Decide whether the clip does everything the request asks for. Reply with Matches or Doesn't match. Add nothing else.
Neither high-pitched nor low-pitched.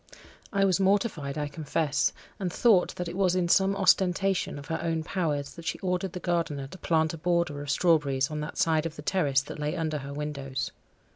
Matches